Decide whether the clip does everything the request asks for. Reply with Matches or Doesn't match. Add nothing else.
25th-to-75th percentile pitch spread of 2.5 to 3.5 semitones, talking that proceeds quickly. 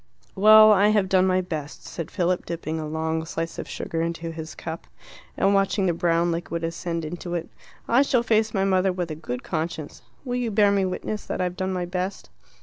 Matches